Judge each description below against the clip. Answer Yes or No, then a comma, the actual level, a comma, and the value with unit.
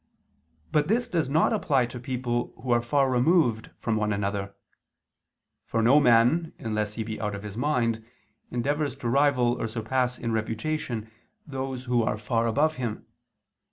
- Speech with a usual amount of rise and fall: Yes, average, 3.9 semitones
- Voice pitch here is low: Yes, low, 120 Hz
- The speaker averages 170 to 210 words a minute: No, average, 160 wpm